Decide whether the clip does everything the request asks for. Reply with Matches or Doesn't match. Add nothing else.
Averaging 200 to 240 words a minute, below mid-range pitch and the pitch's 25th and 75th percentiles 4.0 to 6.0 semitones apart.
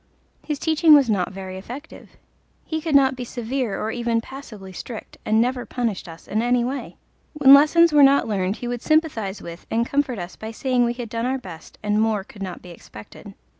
Doesn't match